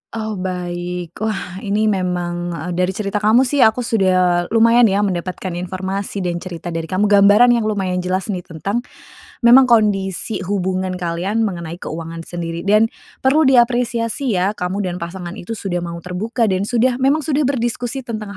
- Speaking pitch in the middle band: No, high, 195 Hz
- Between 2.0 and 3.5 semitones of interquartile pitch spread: No, average, 4.2 semitones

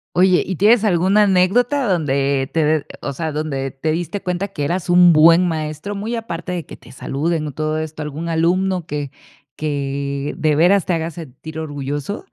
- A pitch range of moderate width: Yes, average, 3.7 semitones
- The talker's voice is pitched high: No, medium, 160 Hz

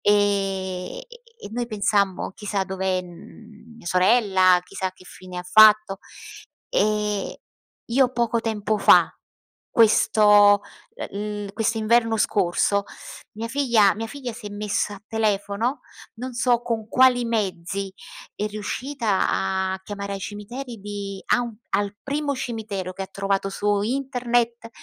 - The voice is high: Yes, high, 210 Hz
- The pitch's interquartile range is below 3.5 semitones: Yes, average, 2.9 semitones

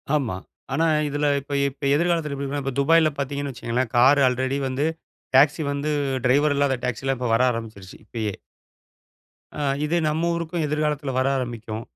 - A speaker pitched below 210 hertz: Yes, medium, 140 Hz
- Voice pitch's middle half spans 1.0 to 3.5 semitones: Yes, average, 3.0 semitones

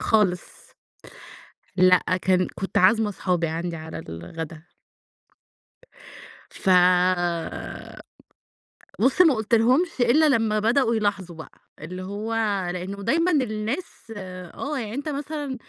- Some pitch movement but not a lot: No, wide, 6.2 semitones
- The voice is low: No, high, 215 Hz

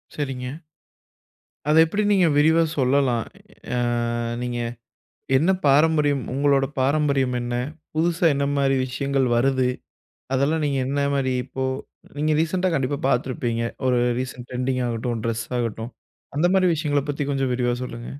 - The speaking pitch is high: No, low, 135 Hz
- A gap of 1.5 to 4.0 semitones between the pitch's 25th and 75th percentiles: Yes, average, 2.9 semitones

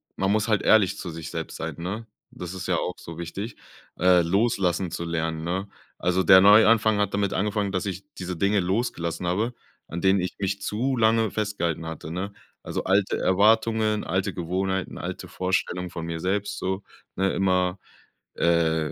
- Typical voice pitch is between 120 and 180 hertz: No, very low, 95 Hz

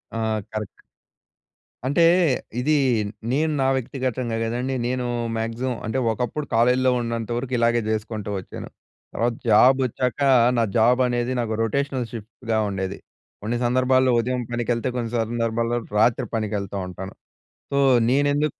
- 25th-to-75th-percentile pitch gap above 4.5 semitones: No, narrow, 2.4 semitones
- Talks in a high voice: No, low, 120 Hz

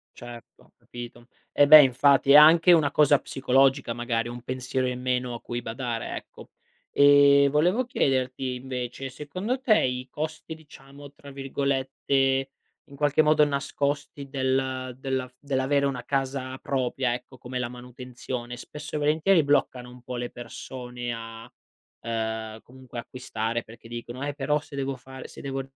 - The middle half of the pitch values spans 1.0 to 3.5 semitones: Yes, narrow, 2.5 semitones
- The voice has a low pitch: Yes, low, 130 Hz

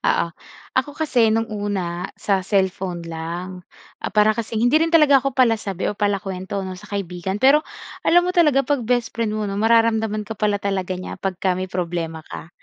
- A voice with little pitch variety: No, average, 3.9 semitones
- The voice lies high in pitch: Yes, high, 205 Hz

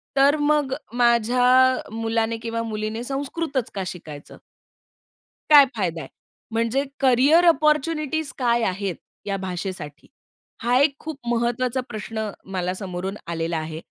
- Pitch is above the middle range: Yes, high, 235 Hz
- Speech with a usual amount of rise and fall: No, wide, 5.8 semitones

